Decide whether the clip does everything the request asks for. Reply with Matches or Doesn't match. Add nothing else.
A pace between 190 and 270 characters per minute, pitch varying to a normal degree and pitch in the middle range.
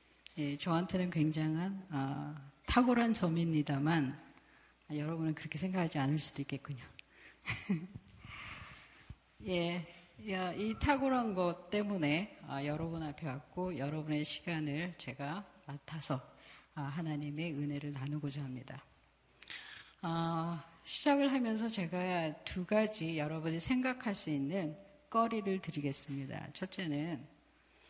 Matches